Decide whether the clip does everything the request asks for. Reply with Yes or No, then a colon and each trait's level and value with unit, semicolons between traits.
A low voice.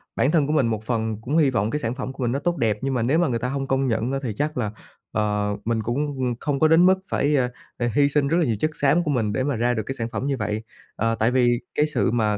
Yes: low, 125 Hz